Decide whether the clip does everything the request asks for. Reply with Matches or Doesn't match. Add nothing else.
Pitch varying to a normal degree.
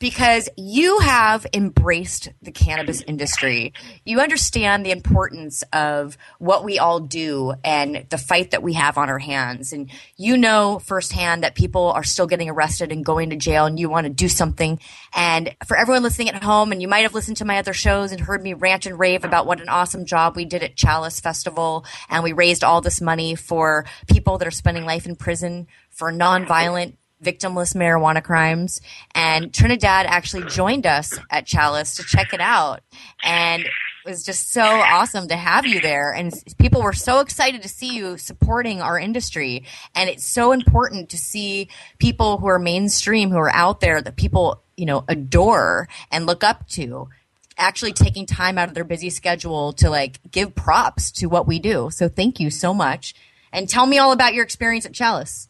Matches